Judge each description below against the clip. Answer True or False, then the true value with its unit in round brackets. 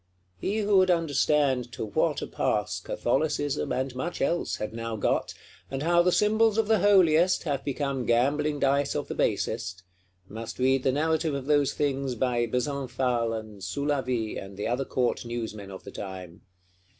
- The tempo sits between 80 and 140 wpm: False (165 wpm)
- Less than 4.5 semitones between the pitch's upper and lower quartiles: False (4.8 semitones)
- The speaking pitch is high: False (135 Hz)